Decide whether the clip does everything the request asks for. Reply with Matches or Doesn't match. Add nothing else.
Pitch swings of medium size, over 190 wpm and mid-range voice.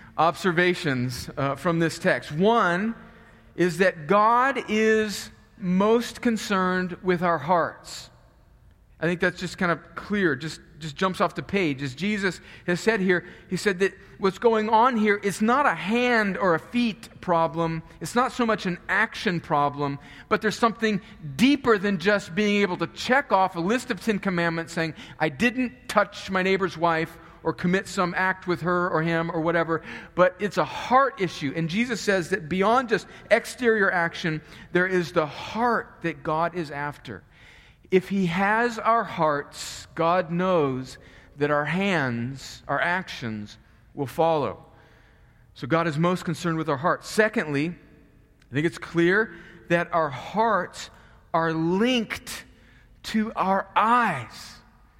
Doesn't match